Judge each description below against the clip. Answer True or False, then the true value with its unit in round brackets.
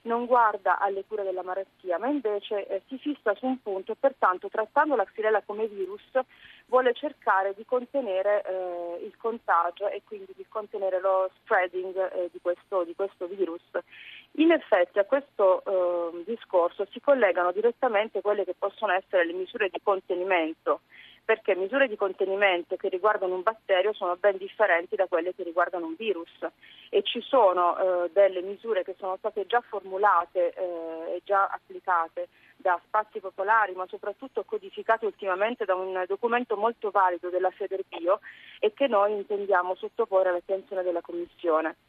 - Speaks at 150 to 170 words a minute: True (160 wpm)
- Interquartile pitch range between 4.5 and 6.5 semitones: False (3.3 semitones)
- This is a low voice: False (200 Hz)